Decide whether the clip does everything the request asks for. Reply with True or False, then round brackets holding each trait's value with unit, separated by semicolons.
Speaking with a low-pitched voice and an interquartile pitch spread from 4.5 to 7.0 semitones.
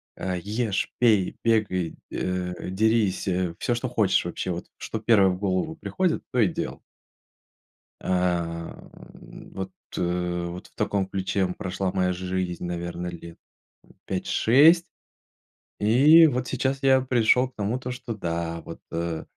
True (95 Hz; 4.9 semitones)